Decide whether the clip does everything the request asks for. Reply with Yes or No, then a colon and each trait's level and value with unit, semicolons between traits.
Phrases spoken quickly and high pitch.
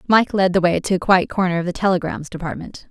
No: fast, 250 wpm; medium, 180 Hz